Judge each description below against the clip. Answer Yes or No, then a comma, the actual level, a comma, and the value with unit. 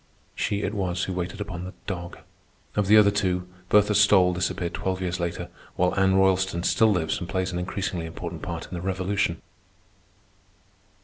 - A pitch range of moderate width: No, narrow, 1.9 semitones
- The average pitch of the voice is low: Yes, very low, 95 Hz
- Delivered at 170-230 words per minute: Yes, average, 175 wpm